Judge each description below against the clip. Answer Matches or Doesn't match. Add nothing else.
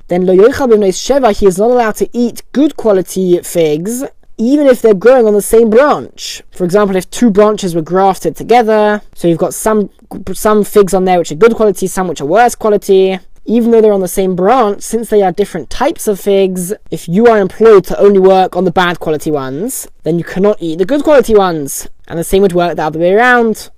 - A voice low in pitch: Doesn't match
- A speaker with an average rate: Doesn't match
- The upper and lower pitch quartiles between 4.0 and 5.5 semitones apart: Doesn't match